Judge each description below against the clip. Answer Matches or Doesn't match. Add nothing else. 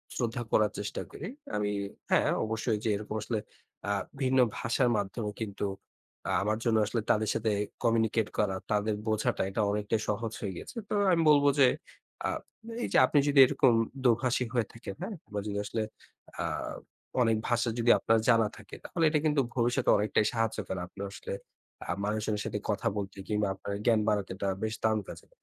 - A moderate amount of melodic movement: Doesn't match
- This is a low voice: Matches